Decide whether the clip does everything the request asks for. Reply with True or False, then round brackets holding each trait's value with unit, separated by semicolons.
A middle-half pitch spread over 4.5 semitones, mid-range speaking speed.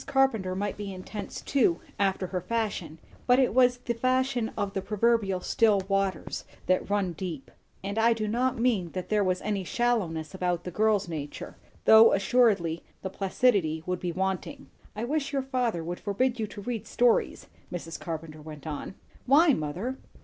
True (4.9 semitones; 170 wpm)